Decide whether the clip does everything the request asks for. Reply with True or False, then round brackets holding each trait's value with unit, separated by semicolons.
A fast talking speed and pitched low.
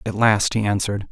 True (215 wpm; 105 Hz)